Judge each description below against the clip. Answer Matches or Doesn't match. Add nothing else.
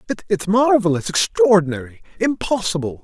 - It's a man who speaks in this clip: Matches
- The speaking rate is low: Matches